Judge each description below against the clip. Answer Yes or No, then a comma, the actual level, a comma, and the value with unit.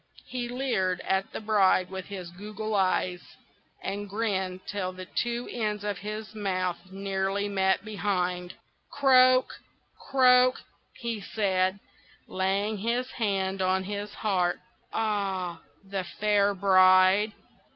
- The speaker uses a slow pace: Yes, slow, 120 wpm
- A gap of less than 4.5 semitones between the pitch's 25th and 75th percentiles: Yes, narrow, 2.4 semitones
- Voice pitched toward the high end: Yes, high, 200 Hz